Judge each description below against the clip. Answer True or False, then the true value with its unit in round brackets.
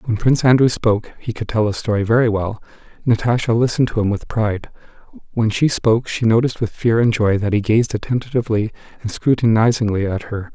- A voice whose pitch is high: False (110 Hz)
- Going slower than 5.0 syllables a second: False (5.5 syllables/s)